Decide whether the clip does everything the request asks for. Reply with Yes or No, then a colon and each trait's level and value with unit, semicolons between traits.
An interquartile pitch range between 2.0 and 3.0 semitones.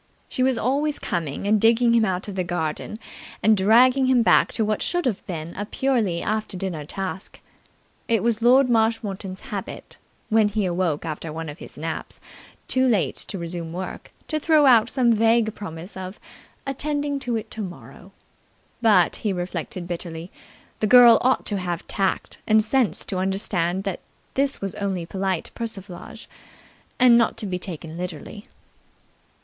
No: average, 4.7 semitones